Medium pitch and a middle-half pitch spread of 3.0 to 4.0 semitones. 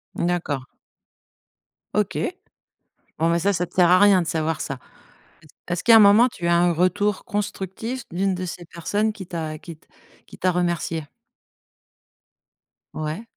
Yes: medium, 175 Hz; average, 3.3 semitones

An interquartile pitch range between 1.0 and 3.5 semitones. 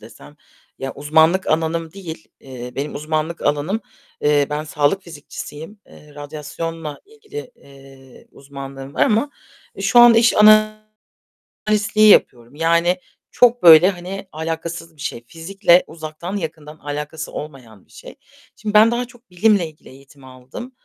No: average, 5.2 semitones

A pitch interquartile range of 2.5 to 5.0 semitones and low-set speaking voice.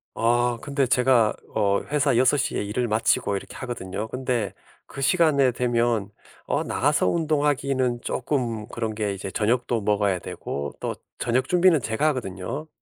Yes: average, 4.2 semitones; low, 120 Hz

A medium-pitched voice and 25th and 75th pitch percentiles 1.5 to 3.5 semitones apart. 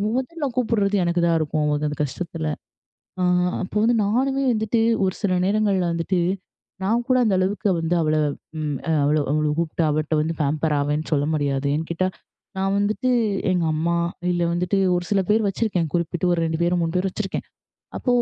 No: medium, 175 Hz; average, 4.5 semitones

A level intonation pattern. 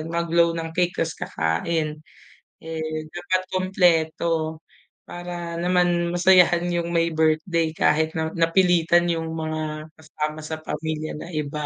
Yes: narrow, 1.6 semitones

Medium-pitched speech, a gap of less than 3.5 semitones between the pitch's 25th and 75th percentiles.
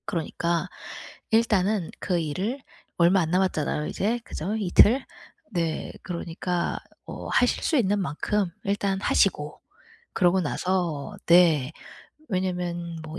Yes: medium, 180 Hz; average, 2.9 semitones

